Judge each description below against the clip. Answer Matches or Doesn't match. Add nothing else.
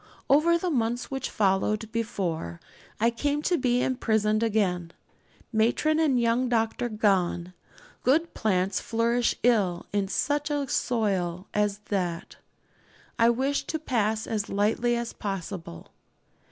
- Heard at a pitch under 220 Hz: Doesn't match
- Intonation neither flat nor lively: Matches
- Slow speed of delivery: Matches